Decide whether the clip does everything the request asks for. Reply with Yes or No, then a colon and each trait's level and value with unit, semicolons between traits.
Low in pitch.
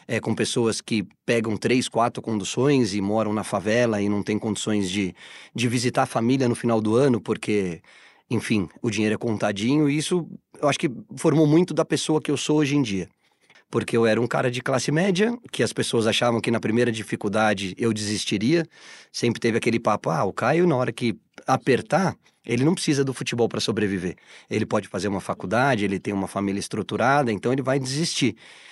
Yes: low, 115 Hz